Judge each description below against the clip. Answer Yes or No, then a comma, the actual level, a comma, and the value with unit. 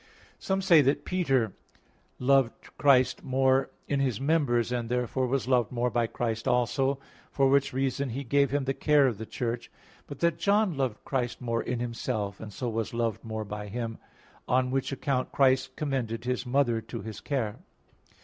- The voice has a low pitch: Yes, low, 125 Hz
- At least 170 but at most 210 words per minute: Yes, average, 180 wpm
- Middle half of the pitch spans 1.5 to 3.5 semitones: Yes, average, 2.9 semitones